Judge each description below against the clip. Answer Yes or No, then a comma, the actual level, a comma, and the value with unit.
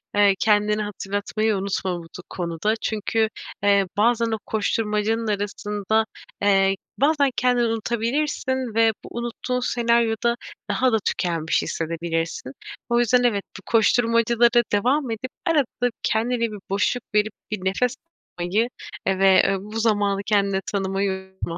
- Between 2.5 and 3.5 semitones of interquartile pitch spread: Yes, average, 3.2 semitones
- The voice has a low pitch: No, high, 215 Hz